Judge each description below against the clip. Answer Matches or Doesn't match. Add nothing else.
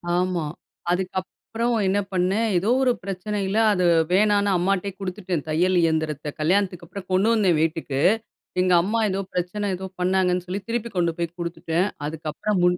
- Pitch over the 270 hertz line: Doesn't match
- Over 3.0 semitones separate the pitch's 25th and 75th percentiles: Doesn't match